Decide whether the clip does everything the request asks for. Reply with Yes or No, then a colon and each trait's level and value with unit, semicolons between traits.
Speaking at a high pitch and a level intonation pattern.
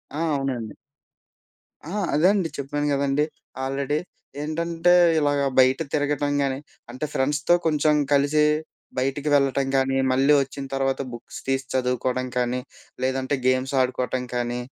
No: low, 135 Hz; narrow, 2.2 semitones